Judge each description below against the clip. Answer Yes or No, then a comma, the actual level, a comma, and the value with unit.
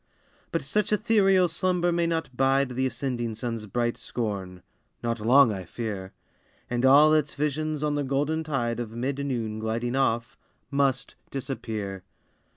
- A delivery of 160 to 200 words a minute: No, average, 150 wpm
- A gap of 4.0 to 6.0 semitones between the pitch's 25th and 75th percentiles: Yes, average, 4.6 semitones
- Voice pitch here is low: Yes, low, 130 Hz